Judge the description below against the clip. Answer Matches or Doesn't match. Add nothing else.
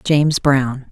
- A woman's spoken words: Matches